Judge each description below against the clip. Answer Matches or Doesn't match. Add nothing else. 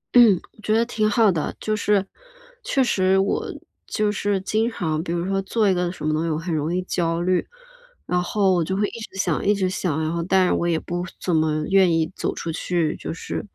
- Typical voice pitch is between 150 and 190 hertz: Matches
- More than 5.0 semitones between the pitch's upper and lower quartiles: Doesn't match